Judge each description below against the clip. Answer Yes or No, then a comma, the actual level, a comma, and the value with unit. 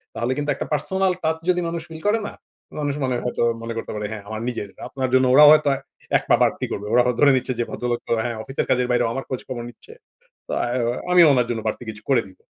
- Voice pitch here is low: Yes, low, 130 Hz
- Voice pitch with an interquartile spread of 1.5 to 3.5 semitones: No, average, 3.9 semitones